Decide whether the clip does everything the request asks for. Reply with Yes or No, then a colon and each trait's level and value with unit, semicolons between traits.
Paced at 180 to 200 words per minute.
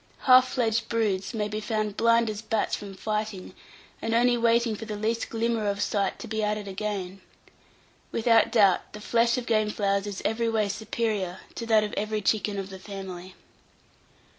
Yes: average, 185 wpm